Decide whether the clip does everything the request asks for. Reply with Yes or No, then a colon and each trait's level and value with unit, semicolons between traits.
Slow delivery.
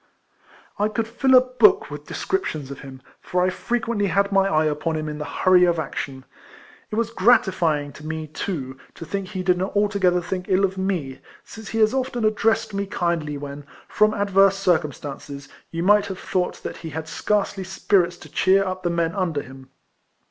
No: average, 190 wpm